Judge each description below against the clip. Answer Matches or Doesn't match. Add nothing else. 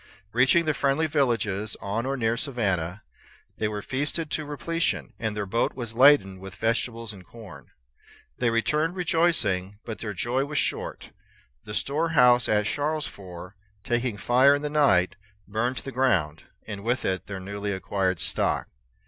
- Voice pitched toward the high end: Doesn't match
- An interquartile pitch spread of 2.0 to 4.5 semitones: Doesn't match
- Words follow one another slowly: Doesn't match